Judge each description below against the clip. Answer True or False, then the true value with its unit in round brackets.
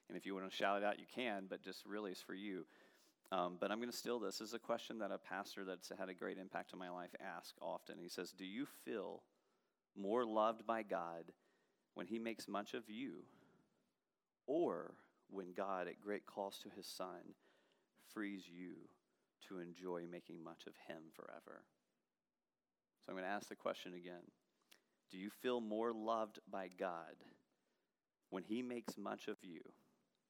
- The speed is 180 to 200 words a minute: True (185 wpm)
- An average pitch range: True (4.0 semitones)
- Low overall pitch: True (100 Hz)